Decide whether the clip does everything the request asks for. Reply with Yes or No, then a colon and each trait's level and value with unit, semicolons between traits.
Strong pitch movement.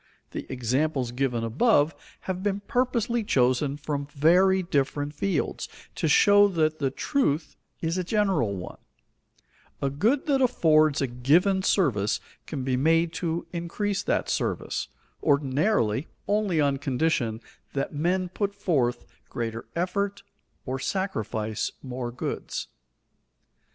Yes: wide, 6.4 semitones